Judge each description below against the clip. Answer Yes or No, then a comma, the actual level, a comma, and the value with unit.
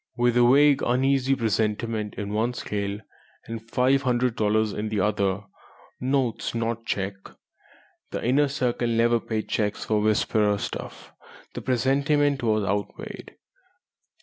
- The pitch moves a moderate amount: Yes, average, 3.2 semitones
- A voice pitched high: No, low, 115 Hz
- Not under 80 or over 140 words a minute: Yes, slow, 135 wpm